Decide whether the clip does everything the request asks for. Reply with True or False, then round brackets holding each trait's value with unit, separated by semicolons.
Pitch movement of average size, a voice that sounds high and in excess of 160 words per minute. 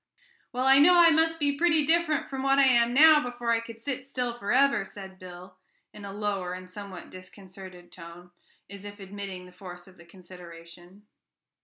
False (6.6 semitones; 205 Hz; 185 wpm)